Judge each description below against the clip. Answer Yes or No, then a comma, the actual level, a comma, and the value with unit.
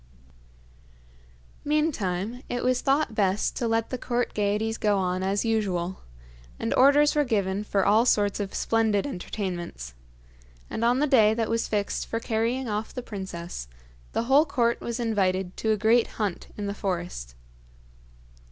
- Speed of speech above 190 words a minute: No, average, 155 wpm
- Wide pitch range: No, average, 3.7 semitones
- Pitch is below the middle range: No, high, 220 Hz